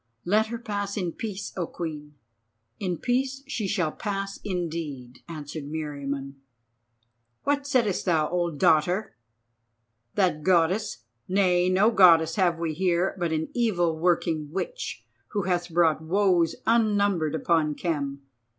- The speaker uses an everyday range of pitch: Yes, average, 4.2 semitones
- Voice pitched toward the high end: No, medium, 175 Hz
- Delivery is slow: Yes, slow, 130 wpm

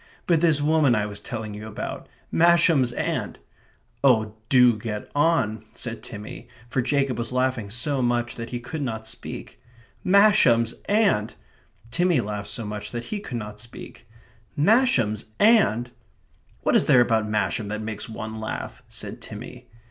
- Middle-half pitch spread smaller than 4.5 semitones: No, average, 5.0 semitones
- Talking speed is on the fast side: No, average, 155 wpm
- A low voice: Yes, low, 120 Hz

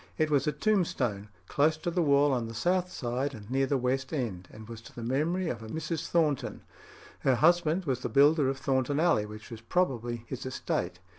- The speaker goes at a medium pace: No, fast, 210 wpm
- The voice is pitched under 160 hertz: Yes, low, 135 Hz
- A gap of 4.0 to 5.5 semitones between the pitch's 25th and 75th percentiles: Yes, average, 4.8 semitones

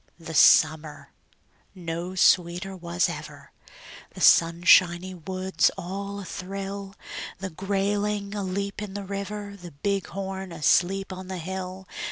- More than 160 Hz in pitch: Yes, high, 190 Hz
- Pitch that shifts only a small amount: Yes, narrow, 2.1 semitones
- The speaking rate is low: Yes, slow, 115 wpm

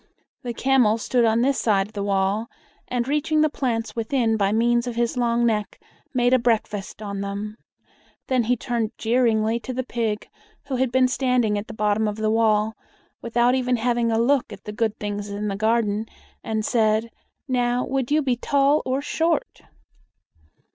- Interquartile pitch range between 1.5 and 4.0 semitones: Yes, average, 2.8 semitones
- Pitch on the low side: No, high, 230 Hz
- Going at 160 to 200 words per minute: Yes, average, 180 wpm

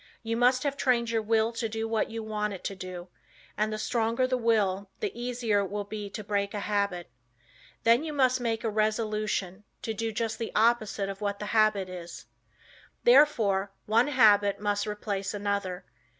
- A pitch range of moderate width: No, narrow, 2.3 semitones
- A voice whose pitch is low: No, high, 215 Hz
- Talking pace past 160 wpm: Yes, average, 185 wpm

